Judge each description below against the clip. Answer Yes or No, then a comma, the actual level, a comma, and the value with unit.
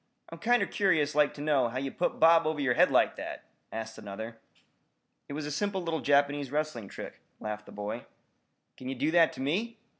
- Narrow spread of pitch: No, average, 4.7 semitones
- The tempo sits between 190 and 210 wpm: Yes, fast, 205 wpm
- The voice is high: No, medium, 145 Hz